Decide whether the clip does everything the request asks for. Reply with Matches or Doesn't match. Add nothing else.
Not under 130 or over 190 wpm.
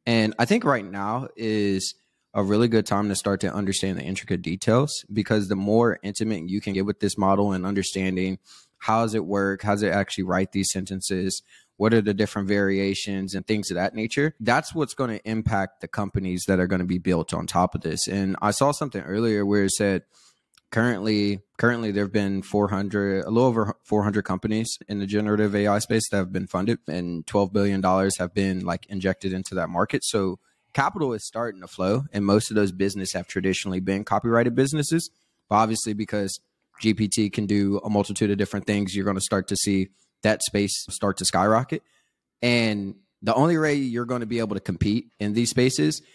Doesn't match